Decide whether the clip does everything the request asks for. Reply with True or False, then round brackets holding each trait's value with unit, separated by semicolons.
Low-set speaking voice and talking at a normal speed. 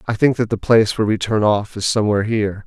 False (110 Hz; 270 wpm)